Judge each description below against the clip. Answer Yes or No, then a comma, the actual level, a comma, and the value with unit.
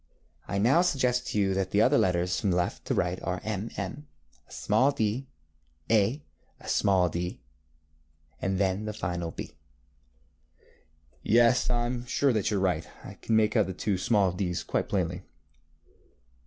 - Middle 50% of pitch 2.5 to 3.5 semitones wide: No, average, 4.6 semitones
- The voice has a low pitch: Yes, low, 100 Hz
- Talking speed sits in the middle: Yes, average, 170 wpm